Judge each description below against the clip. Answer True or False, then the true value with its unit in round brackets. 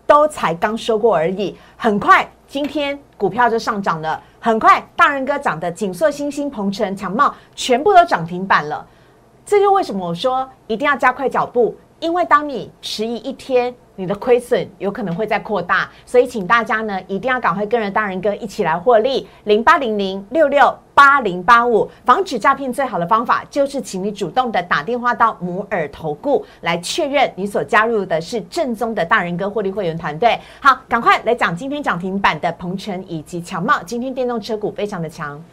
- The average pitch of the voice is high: True (230 Hz)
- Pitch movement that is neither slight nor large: False (5.8 semitones)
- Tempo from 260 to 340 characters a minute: True (295 characters per minute)